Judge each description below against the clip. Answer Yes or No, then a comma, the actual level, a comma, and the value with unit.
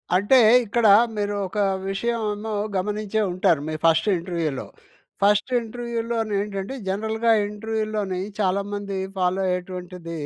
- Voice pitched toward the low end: No, high, 205 Hz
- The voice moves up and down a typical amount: Yes, average, 3.1 semitones